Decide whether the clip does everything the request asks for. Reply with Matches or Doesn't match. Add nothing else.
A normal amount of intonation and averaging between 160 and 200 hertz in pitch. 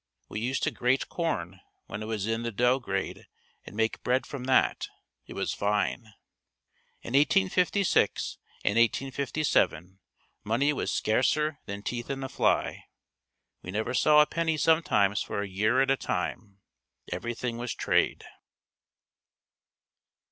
Doesn't match